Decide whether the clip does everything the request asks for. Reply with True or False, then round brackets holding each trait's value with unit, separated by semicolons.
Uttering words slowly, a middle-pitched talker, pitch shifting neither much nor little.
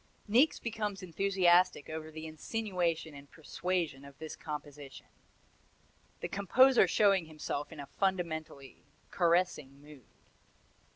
True (110 wpm; 165 Hz; 4.4 semitones)